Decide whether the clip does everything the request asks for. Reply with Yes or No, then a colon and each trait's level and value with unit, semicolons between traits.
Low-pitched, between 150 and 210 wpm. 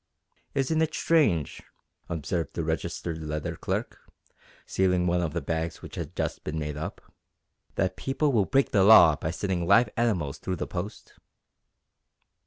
Yes: very low, 90 Hz; average, 155 wpm